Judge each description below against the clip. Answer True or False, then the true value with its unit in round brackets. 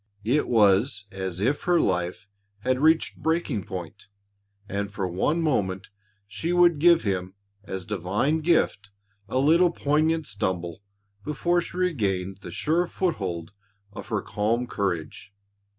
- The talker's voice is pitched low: True (105 Hz)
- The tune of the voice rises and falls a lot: True (8.9 semitones)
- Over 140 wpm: False (135 wpm)